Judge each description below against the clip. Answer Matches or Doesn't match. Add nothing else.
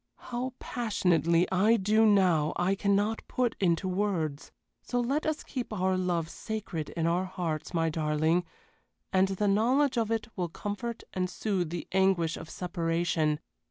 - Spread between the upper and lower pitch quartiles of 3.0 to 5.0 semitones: Matches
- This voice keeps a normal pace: Matches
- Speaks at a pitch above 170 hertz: Matches